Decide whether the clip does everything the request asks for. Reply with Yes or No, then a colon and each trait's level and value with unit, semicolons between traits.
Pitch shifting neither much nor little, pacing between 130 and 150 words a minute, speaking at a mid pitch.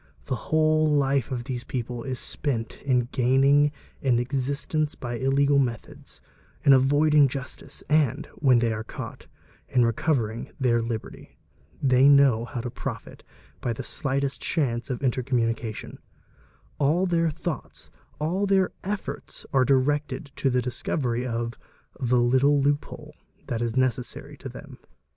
No: average, 3.1 semitones; average, 145 wpm; low, 130 Hz